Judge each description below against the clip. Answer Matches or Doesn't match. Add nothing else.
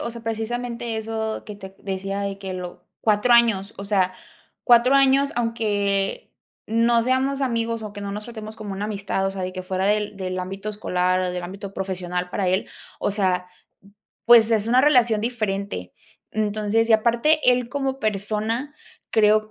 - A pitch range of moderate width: Matches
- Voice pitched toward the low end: Doesn't match